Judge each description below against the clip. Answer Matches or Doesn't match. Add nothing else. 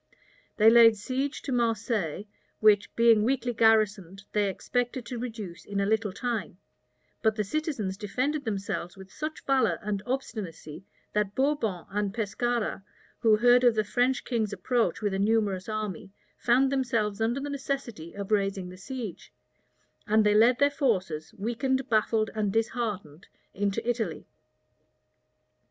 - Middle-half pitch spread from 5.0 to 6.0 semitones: Doesn't match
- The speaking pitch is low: Doesn't match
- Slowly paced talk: Doesn't match